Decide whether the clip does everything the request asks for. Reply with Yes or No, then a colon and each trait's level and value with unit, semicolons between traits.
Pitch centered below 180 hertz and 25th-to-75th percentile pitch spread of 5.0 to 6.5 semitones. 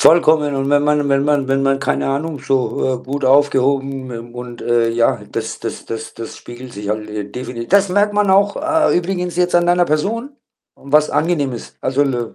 Yes: medium, 140 Hz; wide, 5.6 semitones